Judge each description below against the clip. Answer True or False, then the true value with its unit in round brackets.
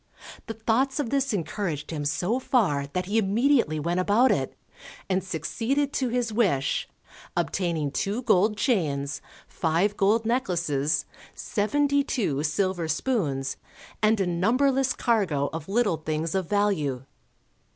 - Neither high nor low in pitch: False (195 Hz)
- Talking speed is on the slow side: True (130 wpm)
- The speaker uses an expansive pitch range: True (6.8 semitones)